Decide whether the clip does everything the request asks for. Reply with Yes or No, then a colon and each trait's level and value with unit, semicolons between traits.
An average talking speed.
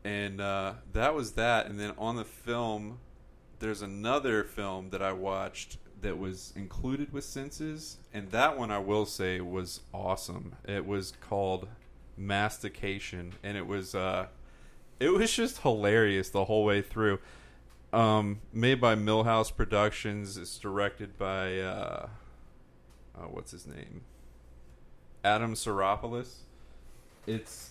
No: slow, 130 wpm